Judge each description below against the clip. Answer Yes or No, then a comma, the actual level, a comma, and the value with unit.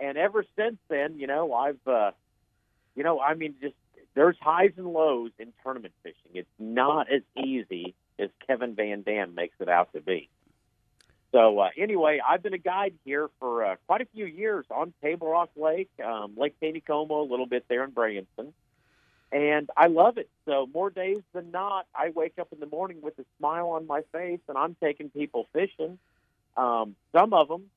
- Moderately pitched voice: Yes, medium, 150 Hz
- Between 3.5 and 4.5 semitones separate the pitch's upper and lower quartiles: No, average, 5.2 semitones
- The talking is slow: No, average, 195 wpm